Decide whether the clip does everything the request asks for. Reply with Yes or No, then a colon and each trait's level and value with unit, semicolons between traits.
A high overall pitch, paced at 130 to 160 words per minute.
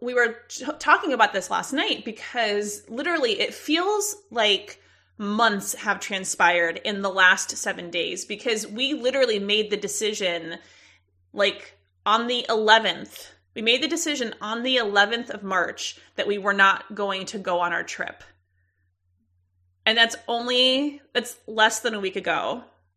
Yes: high, 210 Hz; average, 155 wpm